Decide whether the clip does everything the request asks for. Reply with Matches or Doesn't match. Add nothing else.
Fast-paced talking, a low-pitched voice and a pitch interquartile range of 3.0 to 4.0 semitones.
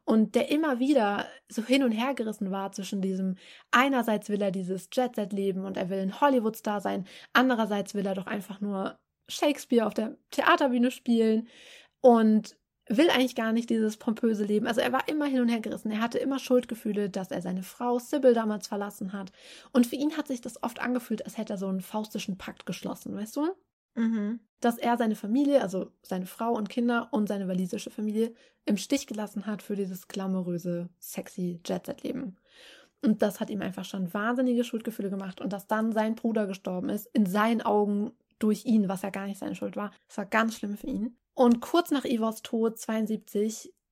Doesn't match